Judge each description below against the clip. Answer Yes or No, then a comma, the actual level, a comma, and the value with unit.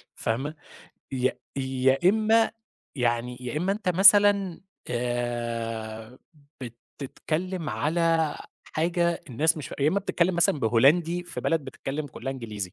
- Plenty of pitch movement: Yes, wide, 6.1 semitones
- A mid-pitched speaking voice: Yes, medium, 145 Hz